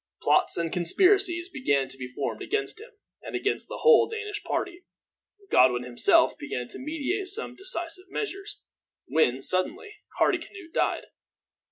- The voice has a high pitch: Yes, very high, 350 Hz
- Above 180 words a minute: No, average, 140 wpm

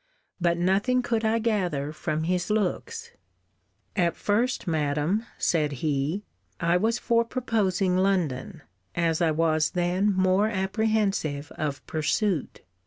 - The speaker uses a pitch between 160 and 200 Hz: Yes, medium, 185 Hz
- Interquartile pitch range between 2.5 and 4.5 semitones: No, average, 5.3 semitones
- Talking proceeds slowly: Yes, slow, 120 wpm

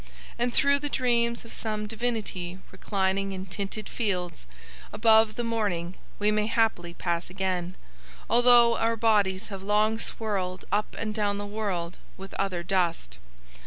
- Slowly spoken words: No, average, 150 wpm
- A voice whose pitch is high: Yes, high, 205 Hz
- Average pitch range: Yes, average, 3.3 semitones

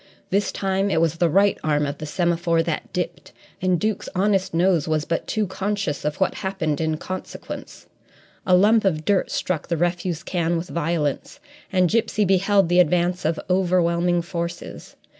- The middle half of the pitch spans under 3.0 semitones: Yes, narrow, 2.6 semitones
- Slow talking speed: No, average, 170 wpm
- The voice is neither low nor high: Yes, medium, 175 Hz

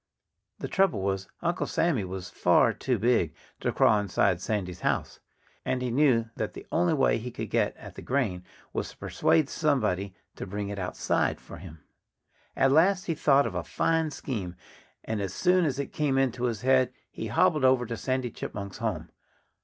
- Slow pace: No, average, 185 wpm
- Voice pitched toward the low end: Yes, low, 125 Hz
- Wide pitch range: Yes, wide, 6.2 semitones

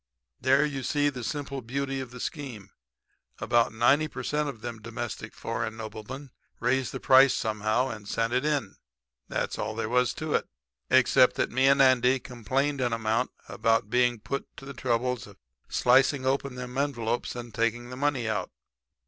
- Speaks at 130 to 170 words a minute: No, average, 180 wpm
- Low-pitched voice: Yes, low, 125 Hz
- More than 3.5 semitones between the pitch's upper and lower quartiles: No, average, 2.8 semitones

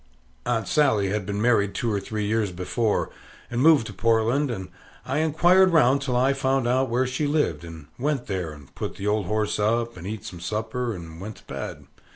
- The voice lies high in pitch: No, low, 115 Hz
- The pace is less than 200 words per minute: No, fast, 205 wpm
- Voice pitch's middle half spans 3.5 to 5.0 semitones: Yes, average, 4.7 semitones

